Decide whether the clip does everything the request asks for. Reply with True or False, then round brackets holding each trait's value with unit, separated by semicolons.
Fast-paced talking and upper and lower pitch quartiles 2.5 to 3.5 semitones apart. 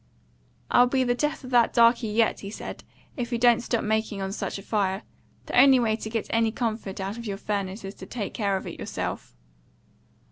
True (215 wpm; 3.1 semitones)